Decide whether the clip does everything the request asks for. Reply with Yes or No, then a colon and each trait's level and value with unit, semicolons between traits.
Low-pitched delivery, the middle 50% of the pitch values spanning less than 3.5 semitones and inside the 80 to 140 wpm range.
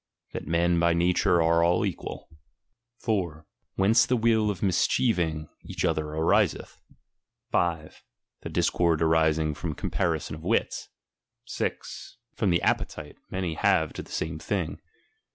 Yes: very low, 85 Hz; average, 3.0 semitones; slow, 135 wpm